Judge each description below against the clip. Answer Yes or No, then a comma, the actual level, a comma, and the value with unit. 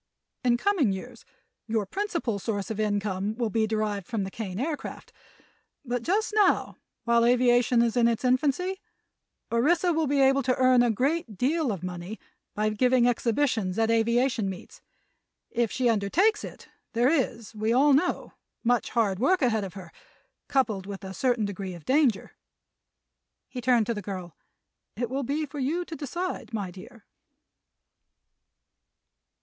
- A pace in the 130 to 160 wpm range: Yes, average, 155 wpm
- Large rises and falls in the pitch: No, average, 4.4 semitones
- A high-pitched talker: Yes, high, 235 Hz